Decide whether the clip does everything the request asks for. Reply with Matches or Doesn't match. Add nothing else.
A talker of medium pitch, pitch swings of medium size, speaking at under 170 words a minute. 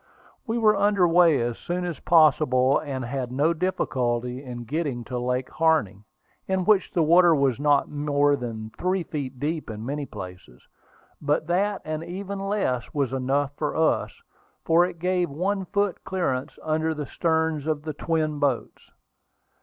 Matches